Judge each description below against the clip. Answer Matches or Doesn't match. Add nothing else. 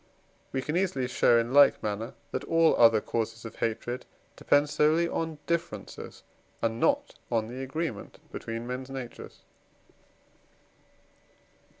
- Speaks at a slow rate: Matches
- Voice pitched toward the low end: Matches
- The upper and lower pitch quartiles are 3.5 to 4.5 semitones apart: Doesn't match